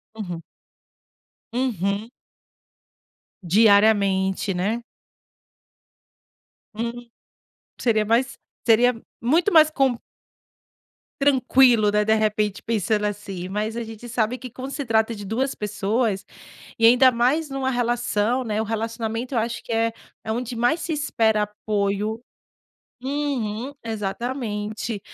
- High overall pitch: Yes, high, 225 Hz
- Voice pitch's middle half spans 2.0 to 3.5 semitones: Yes, average, 3.0 semitones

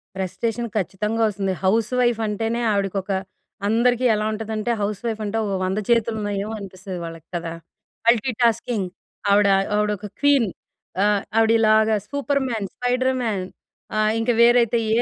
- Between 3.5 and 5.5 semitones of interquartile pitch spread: No, average, 2.7 semitones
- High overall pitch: Yes, high, 220 Hz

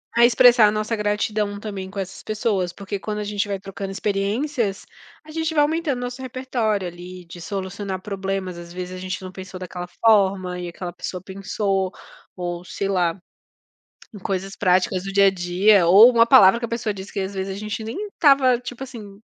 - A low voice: No, high, 200 Hz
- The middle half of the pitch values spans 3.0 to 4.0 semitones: Yes, average, 3.3 semitones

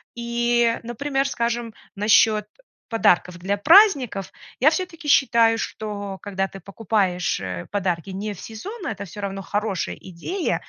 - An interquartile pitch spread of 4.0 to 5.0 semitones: No, average, 3.6 semitones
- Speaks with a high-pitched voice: Yes, high, 215 Hz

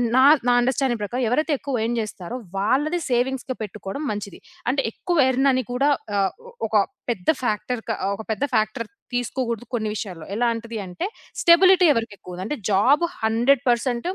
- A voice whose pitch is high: Yes, high, 240 Hz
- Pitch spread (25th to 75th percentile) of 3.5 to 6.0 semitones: Yes, average, 3.8 semitones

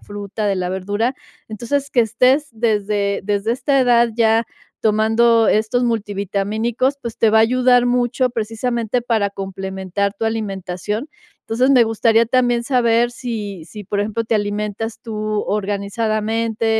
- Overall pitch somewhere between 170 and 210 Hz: No, high, 225 Hz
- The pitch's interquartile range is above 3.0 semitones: No, average, 2.7 semitones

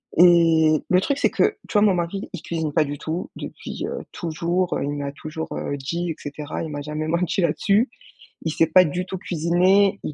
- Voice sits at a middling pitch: Yes, medium, 170 Hz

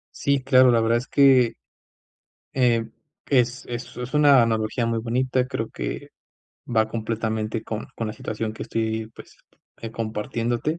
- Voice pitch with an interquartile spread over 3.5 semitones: No, narrow, 2.4 semitones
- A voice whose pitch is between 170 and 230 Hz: No, low, 115 Hz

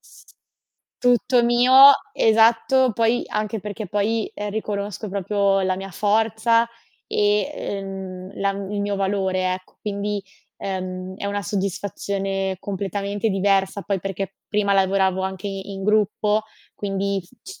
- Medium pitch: No, high, 200 Hz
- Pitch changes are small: Yes, narrow, 1.7 semitones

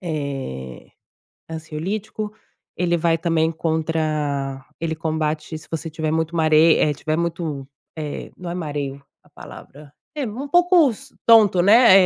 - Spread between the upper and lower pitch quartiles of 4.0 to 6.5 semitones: No, average, 2.8 semitones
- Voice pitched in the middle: Yes, medium, 160 Hz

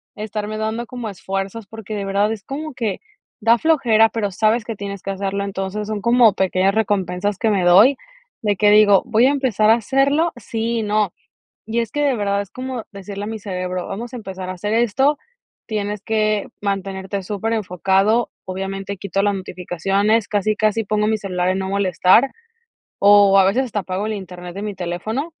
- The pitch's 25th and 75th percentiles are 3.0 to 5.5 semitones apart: No, narrow, 2.5 semitones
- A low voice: No, high, 205 Hz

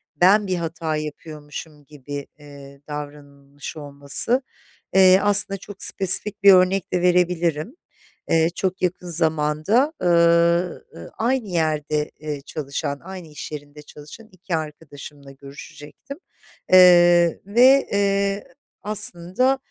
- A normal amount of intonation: Yes, average, 4.4 semitones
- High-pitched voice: No, medium, 170 Hz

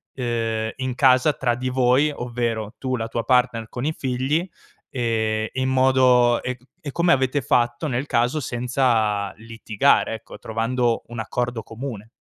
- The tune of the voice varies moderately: No, narrow, 2.3 semitones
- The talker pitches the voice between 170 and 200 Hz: No, low, 125 Hz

